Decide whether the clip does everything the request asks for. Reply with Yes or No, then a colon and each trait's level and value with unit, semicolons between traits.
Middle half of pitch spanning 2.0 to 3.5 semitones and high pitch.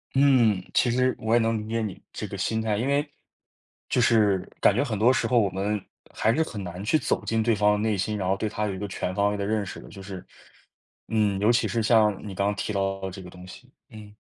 No: narrow, 2.6 semitones; low, 105 Hz